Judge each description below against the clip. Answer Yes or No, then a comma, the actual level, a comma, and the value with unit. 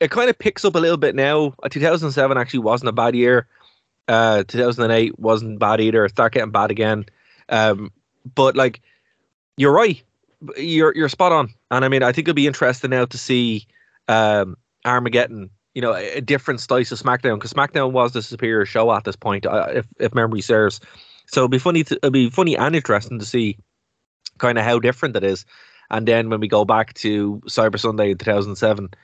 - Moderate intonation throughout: Yes, average, 3.5 semitones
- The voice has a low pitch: Yes, low, 120 Hz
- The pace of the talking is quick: Yes, fast, 215 wpm